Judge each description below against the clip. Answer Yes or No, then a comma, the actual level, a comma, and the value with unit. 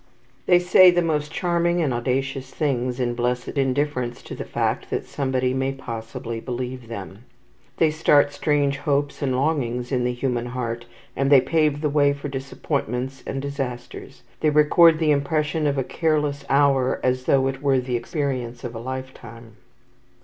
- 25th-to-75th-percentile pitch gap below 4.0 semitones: Yes, average, 2.9 semitones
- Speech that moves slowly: No, average, 165 wpm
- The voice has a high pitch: No, low, 135 Hz